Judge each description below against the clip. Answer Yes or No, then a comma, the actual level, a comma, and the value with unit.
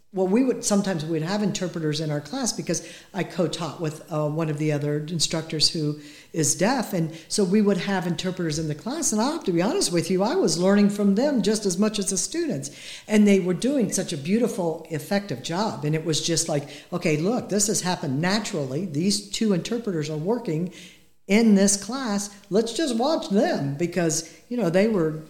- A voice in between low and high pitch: Yes, medium, 180 Hz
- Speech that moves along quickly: Yes, fast, 210 wpm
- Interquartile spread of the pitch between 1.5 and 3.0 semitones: No, average, 4.4 semitones